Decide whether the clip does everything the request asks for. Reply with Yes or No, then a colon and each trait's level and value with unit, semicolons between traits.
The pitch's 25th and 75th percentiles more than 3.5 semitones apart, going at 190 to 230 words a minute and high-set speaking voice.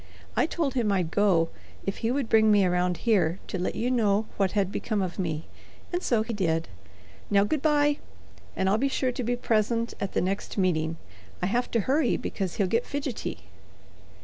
Yes: average, 4.7 semitones; average, 200 wpm; high, 210 Hz